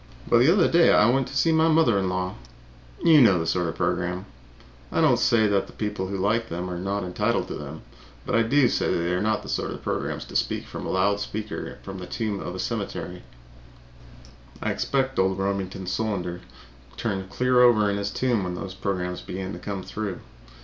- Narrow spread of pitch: No, average, 4.2 semitones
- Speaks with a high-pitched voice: No, low, 100 Hz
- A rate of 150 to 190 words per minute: No, fast, 205 wpm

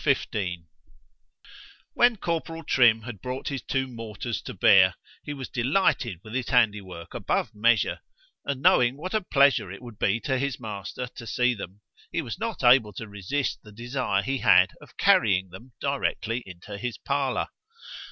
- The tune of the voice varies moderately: Yes, average, 4.8 semitones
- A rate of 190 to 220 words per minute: No, average, 170 wpm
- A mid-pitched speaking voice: No, low, 120 Hz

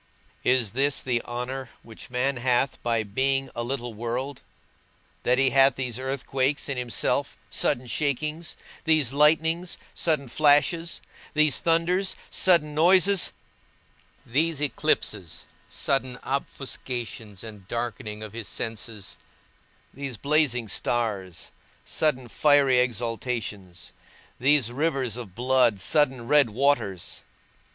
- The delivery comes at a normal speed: No, slow, 110 wpm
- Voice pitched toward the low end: Yes, low, 130 Hz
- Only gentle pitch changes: No, average, 3.8 semitones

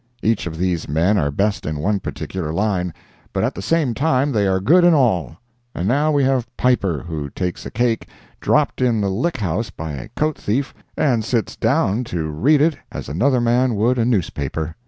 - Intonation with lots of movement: Yes, wide, 6.6 semitones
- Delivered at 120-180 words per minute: No, average, 200 wpm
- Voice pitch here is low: Yes, low, 110 Hz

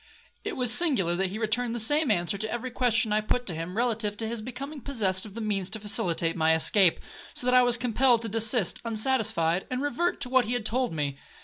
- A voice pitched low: No, high, 225 Hz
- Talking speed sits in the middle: No, fast, 230 wpm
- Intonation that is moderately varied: Yes, average, 4.2 semitones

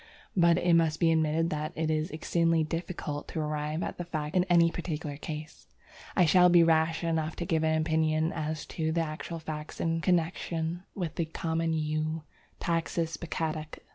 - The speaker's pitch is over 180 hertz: No, medium, 160 Hz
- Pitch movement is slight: Yes, narrow, 1.3 semitones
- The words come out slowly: No, average, 175 wpm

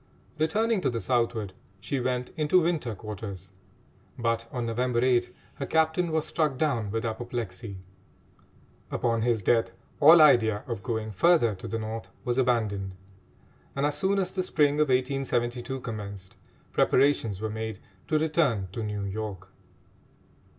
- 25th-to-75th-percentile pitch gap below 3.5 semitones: No, average, 4.9 semitones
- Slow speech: No, average, 145 wpm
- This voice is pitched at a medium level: No, low, 120 Hz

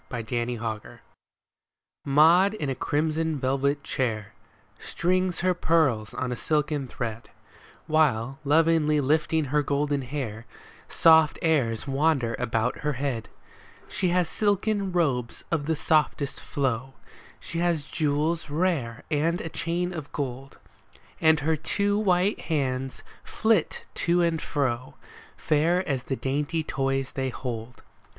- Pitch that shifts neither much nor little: Yes, average, 4.0 semitones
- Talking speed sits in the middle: No, slow, 130 wpm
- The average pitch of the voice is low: No, medium, 150 Hz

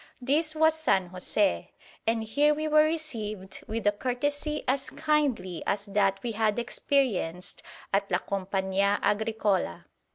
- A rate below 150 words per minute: Yes, slow, 135 wpm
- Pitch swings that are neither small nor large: No, wide, 6.7 semitones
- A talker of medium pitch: No, high, 220 Hz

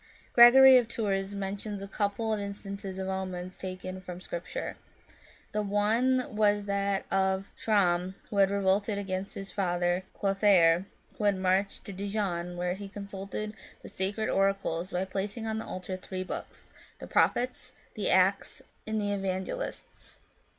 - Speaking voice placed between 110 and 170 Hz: No, high, 195 Hz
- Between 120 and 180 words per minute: Yes, average, 150 wpm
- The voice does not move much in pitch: Yes, narrow, 1.7 semitones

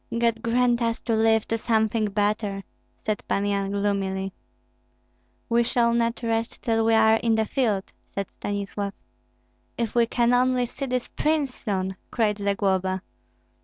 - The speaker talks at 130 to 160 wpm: Yes, average, 150 wpm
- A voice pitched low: No, high, 220 Hz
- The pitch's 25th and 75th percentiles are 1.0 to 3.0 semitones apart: Yes, narrow, 2.6 semitones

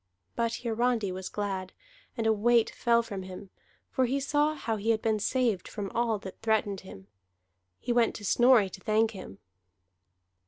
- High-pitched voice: Yes, high, 220 Hz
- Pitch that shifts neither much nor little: Yes, average, 3.1 semitones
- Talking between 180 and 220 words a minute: No, average, 170 wpm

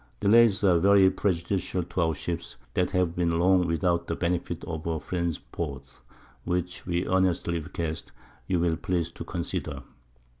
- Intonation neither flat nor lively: No, narrow, 1.8 semitones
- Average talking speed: Yes, average, 155 wpm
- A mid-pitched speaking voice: No, very low, 85 Hz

